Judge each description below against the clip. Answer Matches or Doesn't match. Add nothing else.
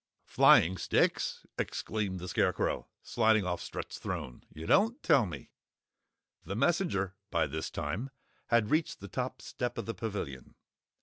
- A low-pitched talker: Matches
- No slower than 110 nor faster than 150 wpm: Matches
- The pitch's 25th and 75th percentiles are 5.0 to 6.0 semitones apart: Matches